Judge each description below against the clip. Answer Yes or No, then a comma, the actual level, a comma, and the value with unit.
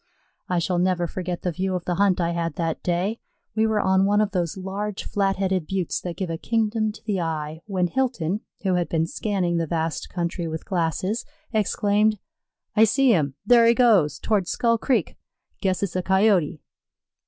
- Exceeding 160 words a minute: Yes, average, 190 wpm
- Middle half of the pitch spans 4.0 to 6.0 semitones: No, average, 3.6 semitones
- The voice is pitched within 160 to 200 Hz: Yes, medium, 185 Hz